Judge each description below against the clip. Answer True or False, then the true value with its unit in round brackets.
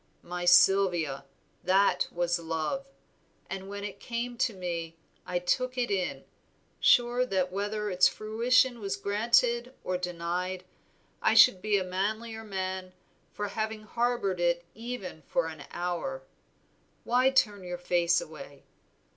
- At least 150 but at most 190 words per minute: False (135 wpm)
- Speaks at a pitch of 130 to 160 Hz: False (195 Hz)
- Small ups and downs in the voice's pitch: False (4.3 semitones)